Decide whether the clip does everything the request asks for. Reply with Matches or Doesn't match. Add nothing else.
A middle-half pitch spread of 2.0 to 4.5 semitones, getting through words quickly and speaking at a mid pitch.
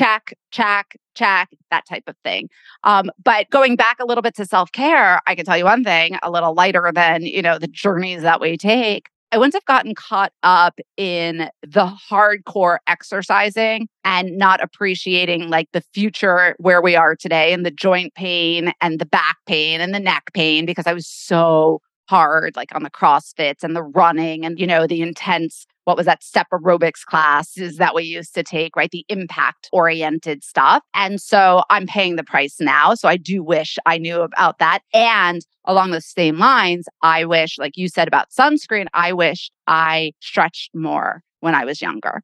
Doesn't match